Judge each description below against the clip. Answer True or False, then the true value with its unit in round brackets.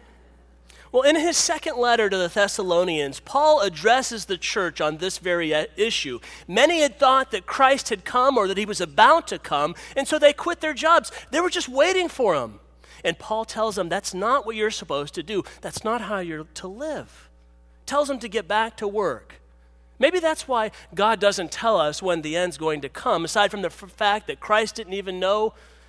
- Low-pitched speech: False (210 Hz)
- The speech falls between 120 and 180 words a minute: False (205 wpm)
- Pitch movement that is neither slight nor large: False (7.4 semitones)